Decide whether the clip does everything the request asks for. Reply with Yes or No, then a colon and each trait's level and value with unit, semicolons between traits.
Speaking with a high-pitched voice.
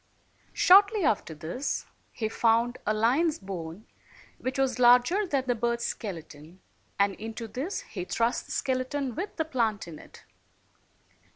Yes: high, 235 Hz